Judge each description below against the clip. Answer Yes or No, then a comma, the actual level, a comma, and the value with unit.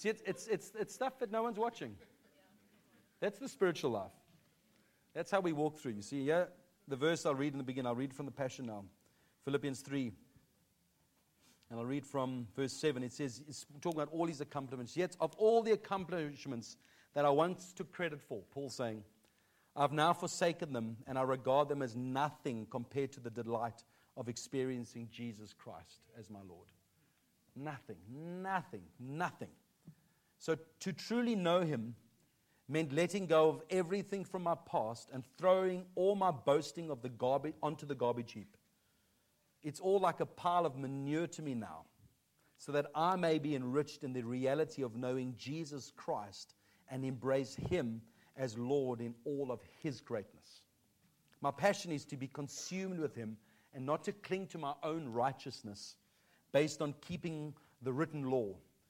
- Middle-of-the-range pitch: Yes, medium, 145 Hz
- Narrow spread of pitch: No, average, 5.1 semitones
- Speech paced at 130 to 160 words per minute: No, average, 170 wpm